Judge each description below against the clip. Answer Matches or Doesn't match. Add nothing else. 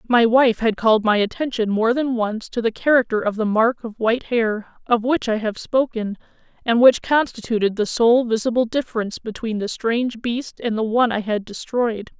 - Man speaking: Doesn't match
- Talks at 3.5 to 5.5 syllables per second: Matches